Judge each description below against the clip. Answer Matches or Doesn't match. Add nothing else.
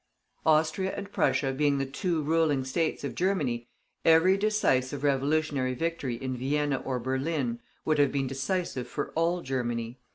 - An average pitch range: Matches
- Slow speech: Doesn't match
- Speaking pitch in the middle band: Matches